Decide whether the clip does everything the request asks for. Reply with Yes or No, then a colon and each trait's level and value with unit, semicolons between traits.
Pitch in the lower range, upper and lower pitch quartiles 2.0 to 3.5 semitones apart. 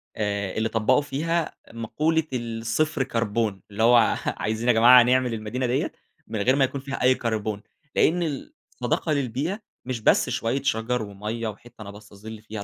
Yes: low, 115 Hz; average, 3.1 semitones